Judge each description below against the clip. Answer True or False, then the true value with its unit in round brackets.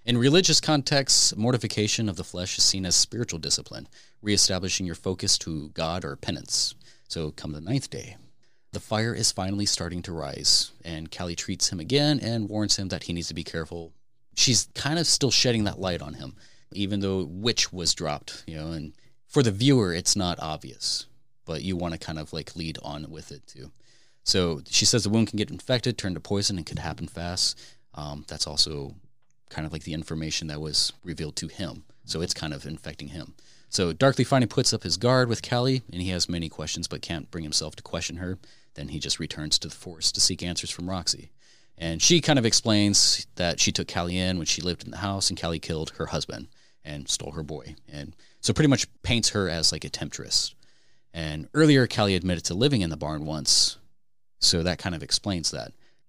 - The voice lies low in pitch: True (90 Hz)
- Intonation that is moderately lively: False (5.7 semitones)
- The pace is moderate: False (210 wpm)